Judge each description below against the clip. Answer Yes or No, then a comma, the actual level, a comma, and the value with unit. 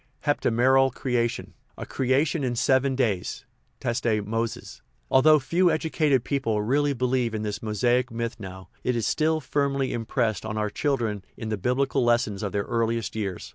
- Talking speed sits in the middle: Yes, average, 165 wpm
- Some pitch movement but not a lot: Yes, average, 3.6 semitones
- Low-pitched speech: Yes, low, 120 Hz